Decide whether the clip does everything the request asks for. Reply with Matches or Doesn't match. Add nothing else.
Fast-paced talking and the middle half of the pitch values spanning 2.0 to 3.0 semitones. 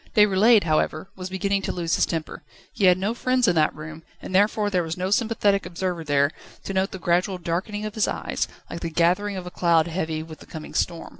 Doesn't match